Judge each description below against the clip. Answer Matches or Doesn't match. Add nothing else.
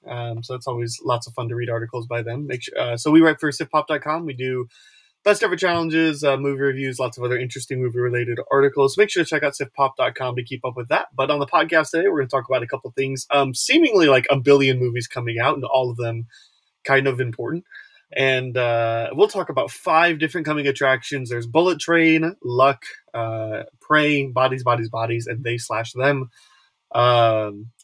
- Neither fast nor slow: Doesn't match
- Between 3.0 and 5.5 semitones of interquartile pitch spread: Matches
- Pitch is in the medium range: Doesn't match